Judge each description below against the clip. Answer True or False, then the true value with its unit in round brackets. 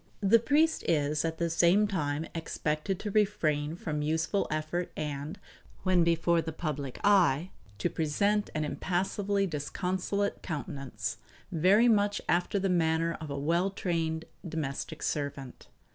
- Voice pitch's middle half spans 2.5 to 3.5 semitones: False (4.2 semitones)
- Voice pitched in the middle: True (165 Hz)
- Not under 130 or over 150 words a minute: True (135 wpm)